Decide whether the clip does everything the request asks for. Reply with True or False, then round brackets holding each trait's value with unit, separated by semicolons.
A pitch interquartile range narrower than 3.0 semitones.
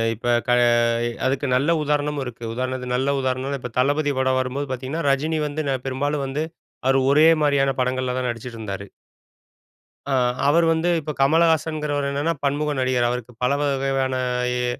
True (2.4 semitones)